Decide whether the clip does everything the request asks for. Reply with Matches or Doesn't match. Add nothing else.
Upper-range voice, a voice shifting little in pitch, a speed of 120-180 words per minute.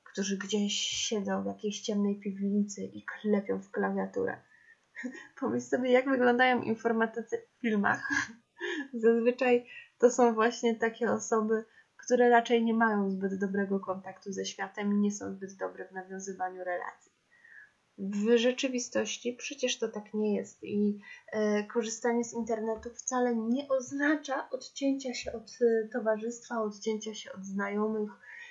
Doesn't match